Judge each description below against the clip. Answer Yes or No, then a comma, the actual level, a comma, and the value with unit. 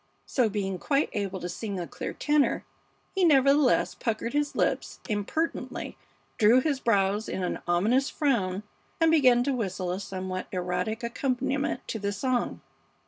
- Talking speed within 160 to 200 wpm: No, average, 150 wpm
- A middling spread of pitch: No, wide, 6.0 semitones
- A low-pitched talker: No, high, 225 Hz